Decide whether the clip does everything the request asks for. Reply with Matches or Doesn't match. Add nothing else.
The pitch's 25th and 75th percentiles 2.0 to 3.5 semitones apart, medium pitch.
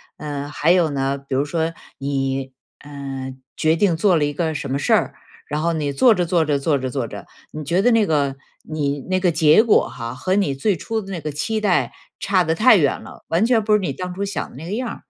Doesn't match